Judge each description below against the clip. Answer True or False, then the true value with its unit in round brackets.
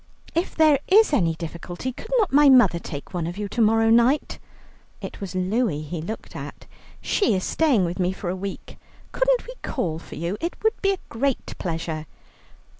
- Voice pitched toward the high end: True (210 Hz)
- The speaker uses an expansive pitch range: True (8.5 semitones)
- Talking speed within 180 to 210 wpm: True (190 wpm)